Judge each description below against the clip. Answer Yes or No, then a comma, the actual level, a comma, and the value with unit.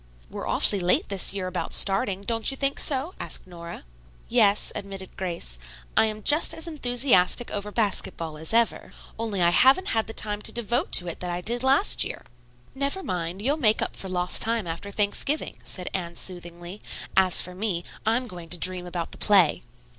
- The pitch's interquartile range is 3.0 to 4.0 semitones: No, average, 4.7 semitones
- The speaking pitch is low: No, high, 200 Hz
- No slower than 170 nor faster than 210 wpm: Yes, average, 190 wpm